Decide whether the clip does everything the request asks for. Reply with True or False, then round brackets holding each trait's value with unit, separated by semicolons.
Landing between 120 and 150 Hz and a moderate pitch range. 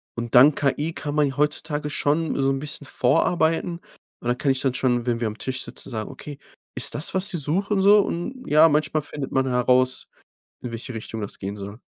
True (140 Hz; 3.8 semitones)